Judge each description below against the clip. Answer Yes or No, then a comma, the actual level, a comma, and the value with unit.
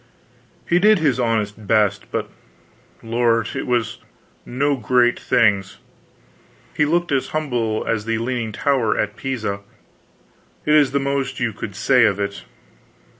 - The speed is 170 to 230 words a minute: No, average, 140 wpm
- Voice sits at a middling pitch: No, low, 120 Hz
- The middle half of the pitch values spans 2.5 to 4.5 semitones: Yes, average, 4.1 semitones